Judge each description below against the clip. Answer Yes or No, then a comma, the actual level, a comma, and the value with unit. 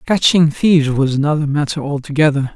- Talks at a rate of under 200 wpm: Yes, average, 140 wpm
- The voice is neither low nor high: Yes, medium, 150 Hz